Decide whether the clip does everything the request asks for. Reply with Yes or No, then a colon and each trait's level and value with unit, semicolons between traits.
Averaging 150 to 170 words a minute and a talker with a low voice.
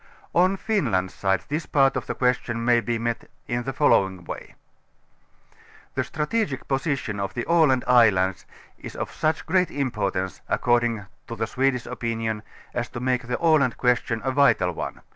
Yes: average, 160 wpm; low, 120 Hz